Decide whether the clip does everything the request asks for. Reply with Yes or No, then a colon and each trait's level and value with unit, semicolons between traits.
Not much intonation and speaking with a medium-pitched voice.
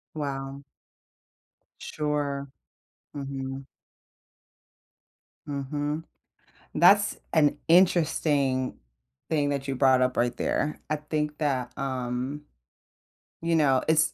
Yes: narrow, 2.2 semitones; medium, 145 Hz